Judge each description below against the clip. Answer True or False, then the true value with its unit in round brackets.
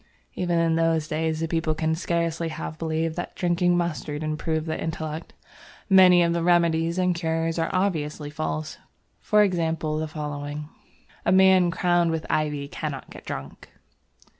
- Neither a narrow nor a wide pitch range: False (1.8 semitones)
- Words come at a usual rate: True (155 wpm)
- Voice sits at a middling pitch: True (165 Hz)